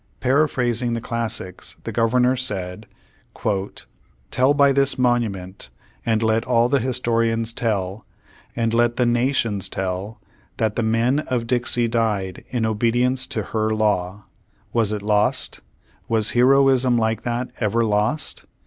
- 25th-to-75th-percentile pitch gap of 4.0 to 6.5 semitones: No, narrow, 2.5 semitones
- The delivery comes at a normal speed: No, slow, 130 wpm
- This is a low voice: Yes, low, 115 Hz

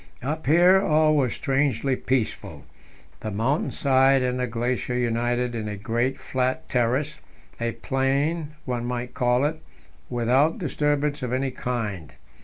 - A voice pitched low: Yes, low, 130 Hz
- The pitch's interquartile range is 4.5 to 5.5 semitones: No, average, 3.1 semitones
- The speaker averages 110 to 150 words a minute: Yes, average, 140 wpm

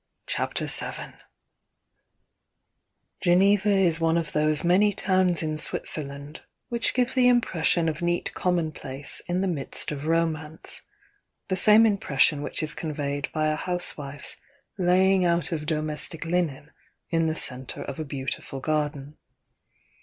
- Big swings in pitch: No, average, 3.4 semitones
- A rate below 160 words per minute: Yes, average, 140 wpm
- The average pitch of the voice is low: No, medium, 165 Hz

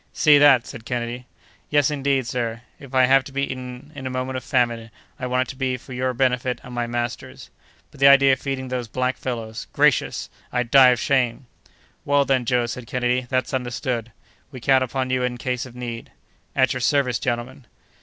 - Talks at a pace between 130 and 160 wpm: No, average, 200 wpm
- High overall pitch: No, low, 125 Hz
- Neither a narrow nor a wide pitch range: No, narrow, 1.5 semitones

